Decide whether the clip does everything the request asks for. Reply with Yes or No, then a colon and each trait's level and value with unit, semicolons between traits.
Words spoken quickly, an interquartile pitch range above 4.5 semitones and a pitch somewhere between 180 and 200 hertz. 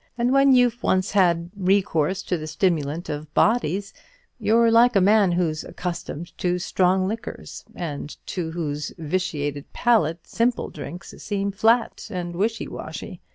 No: average, 145 wpm; average, 4.9 semitones; medium, 185 Hz